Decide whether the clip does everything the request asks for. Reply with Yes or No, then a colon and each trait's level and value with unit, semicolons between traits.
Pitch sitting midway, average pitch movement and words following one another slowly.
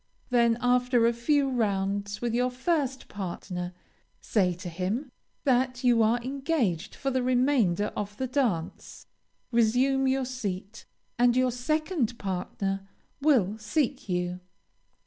No: high, 240 Hz; average, 4.6 semitones; slow, 125 wpm